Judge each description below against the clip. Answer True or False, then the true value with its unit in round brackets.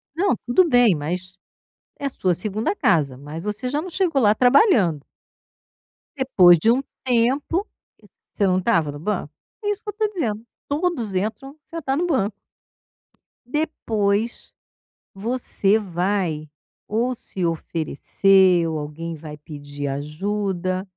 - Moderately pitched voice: False (205 Hz)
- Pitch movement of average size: False (7.7 semitones)